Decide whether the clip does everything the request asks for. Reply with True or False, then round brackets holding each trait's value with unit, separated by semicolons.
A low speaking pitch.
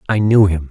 True (95 Hz)